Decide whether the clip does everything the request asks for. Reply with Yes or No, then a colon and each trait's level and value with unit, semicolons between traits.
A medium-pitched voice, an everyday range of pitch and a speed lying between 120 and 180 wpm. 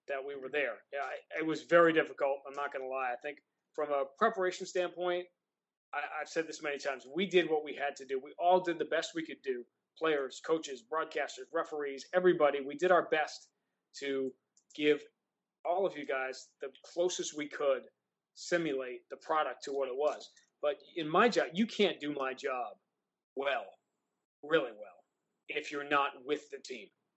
No: medium, 155 Hz; average, 4.2 semitones; average, 190 wpm